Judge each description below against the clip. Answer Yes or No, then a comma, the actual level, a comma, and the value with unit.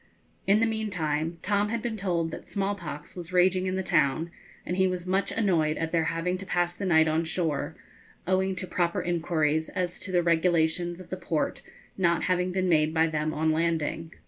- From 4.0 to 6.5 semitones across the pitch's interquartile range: No, narrow, 2.6 semitones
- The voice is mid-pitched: Yes, medium, 175 Hz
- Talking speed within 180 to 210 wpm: Yes, average, 200 wpm